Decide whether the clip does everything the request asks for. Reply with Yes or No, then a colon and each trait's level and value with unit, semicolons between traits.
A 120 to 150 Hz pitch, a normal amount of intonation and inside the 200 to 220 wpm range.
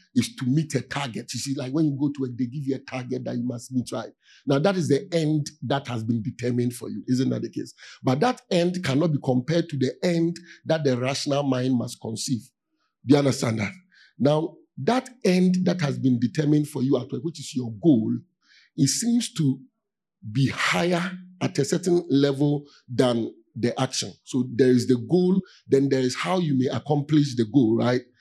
Yes: medium, 140 Hz; average, 4.9 semitones; fast, 205 wpm